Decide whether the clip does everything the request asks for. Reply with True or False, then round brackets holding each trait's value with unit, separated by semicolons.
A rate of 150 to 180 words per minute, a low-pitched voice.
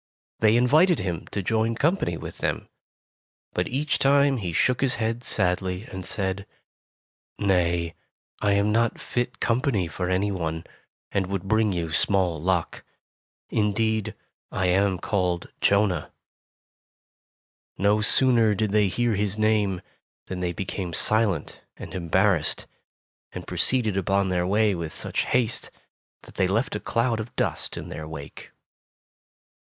False (140 wpm; 100 Hz)